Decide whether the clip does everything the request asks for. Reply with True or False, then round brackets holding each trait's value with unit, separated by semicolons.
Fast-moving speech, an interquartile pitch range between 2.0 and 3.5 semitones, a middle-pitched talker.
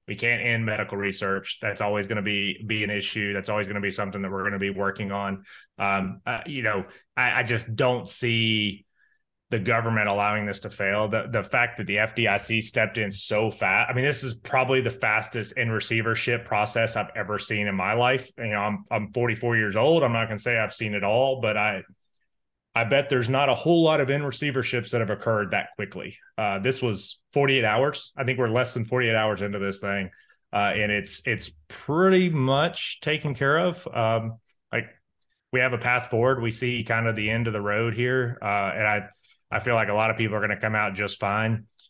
False (225 wpm; 3.2 semitones; 110 Hz)